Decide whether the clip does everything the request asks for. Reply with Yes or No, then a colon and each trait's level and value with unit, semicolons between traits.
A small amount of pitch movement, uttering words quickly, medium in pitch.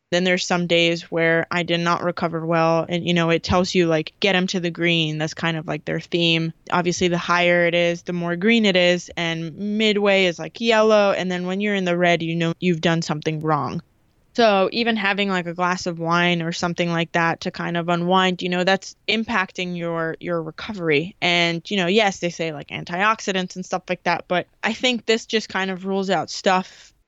Yes: narrow, 2.0 semitones; fast, 225 wpm; medium, 175 Hz